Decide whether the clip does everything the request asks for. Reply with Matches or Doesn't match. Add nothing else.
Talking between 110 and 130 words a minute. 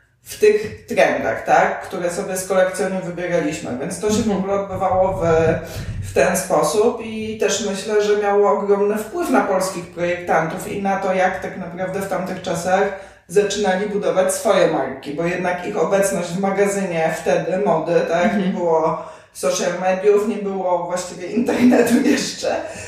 Doesn't match